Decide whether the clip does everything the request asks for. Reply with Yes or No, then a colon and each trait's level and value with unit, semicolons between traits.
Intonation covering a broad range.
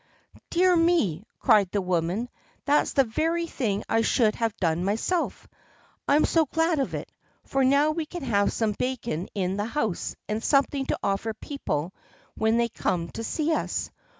Yes: wide, 6.8 semitones